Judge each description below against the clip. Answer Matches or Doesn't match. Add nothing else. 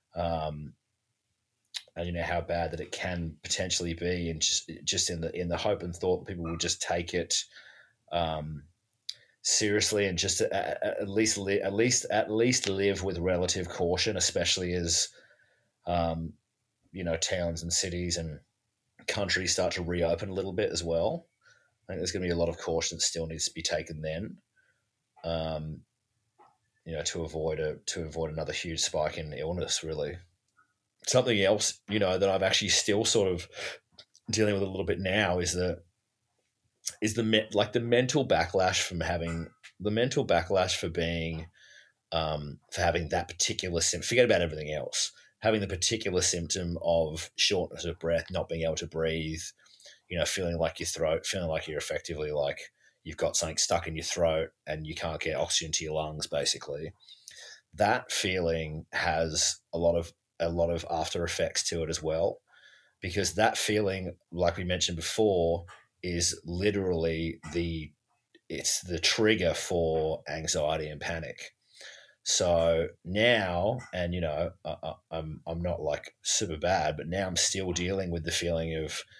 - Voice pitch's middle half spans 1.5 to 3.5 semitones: Matches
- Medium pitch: Doesn't match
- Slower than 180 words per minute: Matches